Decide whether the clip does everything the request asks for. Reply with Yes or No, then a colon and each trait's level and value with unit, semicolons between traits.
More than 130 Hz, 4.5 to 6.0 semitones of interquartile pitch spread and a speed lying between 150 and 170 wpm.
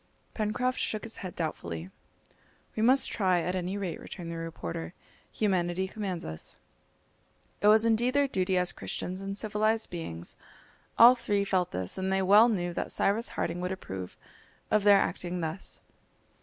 No: high, 190 Hz; average, 3.7 semitones; average, 160 wpm